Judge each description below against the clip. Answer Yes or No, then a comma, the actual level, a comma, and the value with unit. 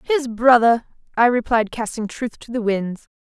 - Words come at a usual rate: Yes, average, 165 wpm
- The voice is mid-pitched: No, high, 235 Hz